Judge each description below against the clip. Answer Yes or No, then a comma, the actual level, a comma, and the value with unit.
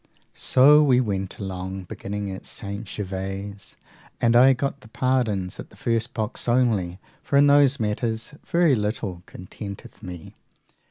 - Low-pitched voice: Yes, low, 110 Hz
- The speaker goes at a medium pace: Yes, average, 145 wpm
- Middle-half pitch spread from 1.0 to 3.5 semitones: No, average, 4.7 semitones